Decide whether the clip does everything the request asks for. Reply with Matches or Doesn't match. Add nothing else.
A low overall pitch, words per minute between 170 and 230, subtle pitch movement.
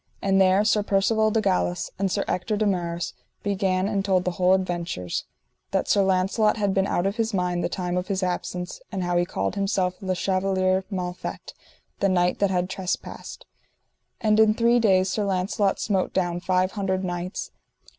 Doesn't match